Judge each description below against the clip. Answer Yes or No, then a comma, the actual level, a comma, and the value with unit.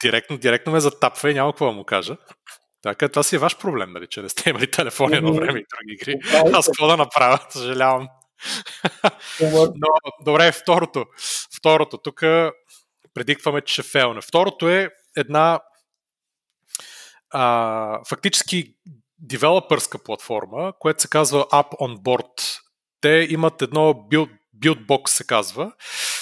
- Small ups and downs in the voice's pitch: No, average, 3.5 semitones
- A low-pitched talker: No, medium, 150 Hz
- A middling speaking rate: Yes, average, 140 wpm